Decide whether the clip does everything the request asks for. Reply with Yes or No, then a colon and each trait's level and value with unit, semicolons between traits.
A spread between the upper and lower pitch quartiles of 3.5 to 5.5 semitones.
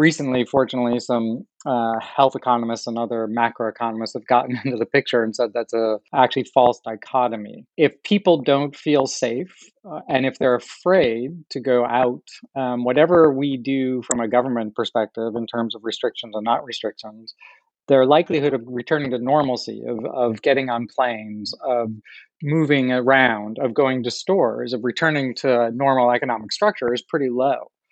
No: average, 2.7 semitones